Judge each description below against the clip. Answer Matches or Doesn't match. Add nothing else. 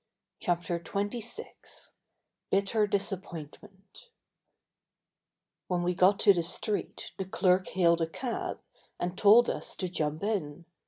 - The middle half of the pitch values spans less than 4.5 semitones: Matches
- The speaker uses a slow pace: Matches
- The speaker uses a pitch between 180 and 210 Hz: Matches